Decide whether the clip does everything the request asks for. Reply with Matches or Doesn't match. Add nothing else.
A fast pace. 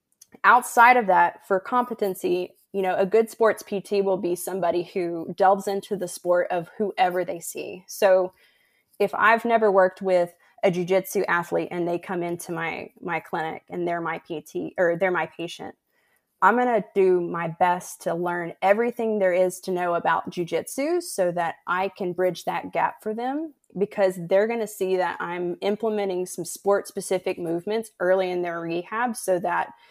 Doesn't match